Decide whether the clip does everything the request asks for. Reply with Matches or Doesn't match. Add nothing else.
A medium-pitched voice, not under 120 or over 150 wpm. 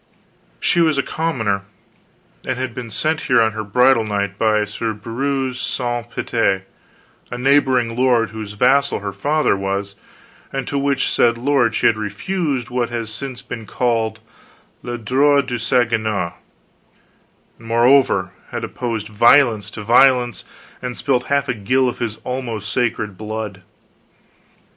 Doesn't match